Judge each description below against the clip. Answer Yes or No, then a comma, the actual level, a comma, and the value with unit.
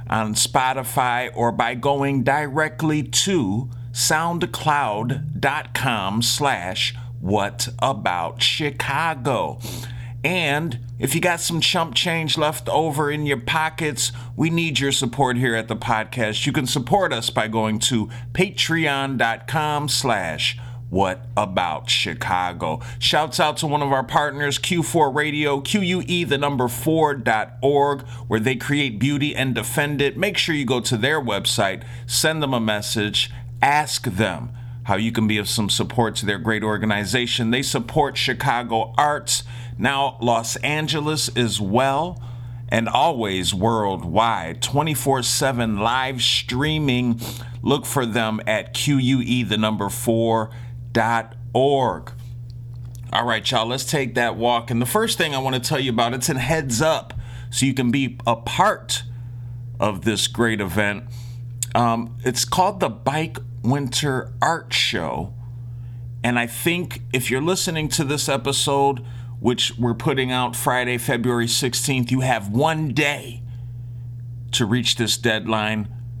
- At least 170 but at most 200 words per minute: No, slow, 135 wpm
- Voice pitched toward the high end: No, low, 125 Hz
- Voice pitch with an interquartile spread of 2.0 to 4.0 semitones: Yes, average, 3.1 semitones